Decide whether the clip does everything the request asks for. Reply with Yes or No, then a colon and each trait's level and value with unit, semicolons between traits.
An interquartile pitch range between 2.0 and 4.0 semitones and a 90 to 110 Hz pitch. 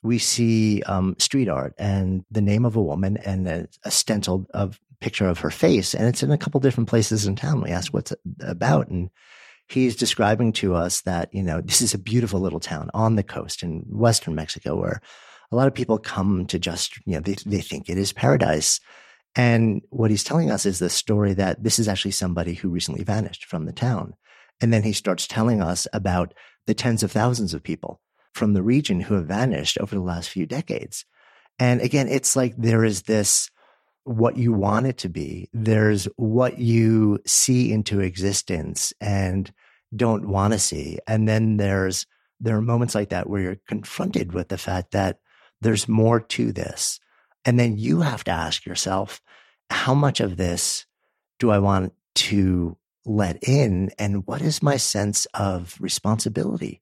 Yes: average, 3.6 semitones; low, 105 Hz